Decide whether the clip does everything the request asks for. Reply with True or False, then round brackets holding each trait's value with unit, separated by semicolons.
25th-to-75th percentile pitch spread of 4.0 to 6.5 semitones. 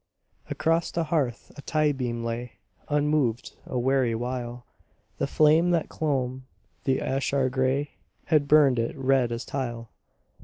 False (3.3 semitones)